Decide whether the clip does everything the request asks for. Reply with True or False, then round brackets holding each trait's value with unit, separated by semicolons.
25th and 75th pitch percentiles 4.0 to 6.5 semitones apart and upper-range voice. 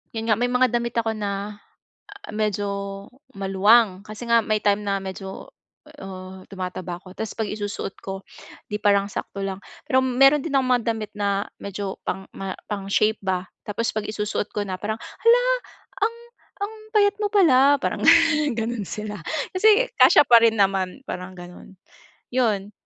False (3.3 semitones; 210 Hz)